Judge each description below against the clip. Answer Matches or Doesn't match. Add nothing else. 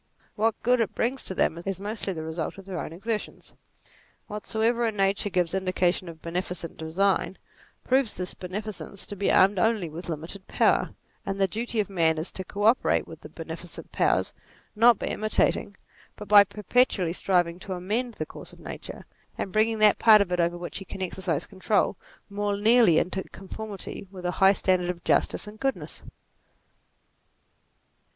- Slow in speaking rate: Doesn't match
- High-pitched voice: Matches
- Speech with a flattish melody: Doesn't match